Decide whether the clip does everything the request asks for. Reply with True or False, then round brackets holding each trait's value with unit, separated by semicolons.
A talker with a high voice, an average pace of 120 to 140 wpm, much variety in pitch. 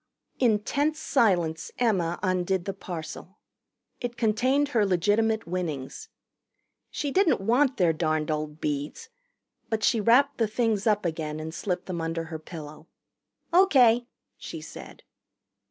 True (195 Hz; 135 wpm; 6.6 semitones)